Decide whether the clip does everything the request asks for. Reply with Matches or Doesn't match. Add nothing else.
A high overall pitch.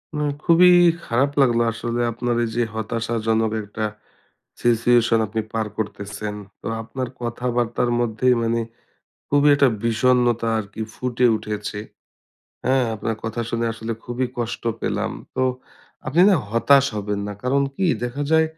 Doesn't match